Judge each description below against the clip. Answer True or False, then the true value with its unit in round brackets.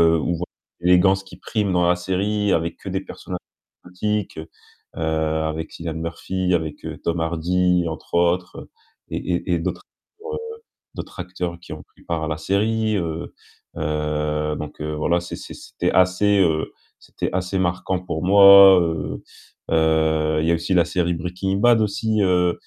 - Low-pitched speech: True (90 Hz)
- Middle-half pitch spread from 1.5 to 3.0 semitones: True (2.7 semitones)